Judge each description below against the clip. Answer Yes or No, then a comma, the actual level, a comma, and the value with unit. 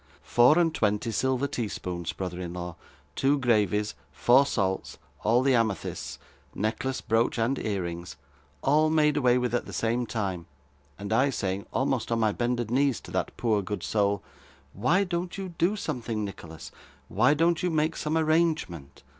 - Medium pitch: No, low, 120 Hz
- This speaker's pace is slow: No, average, 170 wpm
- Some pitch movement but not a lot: No, wide, 5.8 semitones